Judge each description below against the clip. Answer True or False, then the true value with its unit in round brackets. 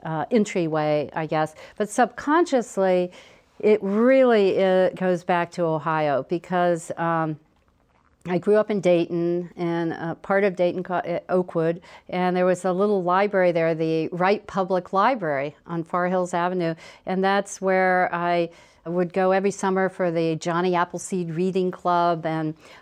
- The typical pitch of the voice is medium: True (180 Hz)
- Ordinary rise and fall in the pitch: False (2.3 semitones)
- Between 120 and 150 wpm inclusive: True (145 wpm)